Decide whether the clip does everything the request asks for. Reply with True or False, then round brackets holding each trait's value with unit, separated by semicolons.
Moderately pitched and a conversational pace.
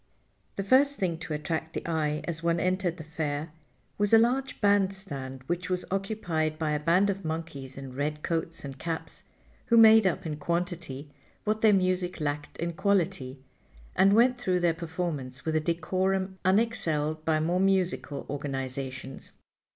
True (170 Hz; 165 wpm)